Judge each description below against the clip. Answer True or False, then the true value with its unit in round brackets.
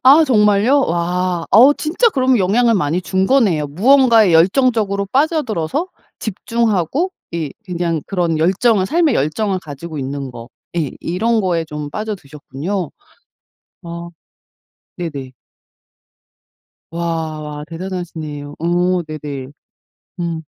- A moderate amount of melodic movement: False (5.8 semitones)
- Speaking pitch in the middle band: True (180 Hz)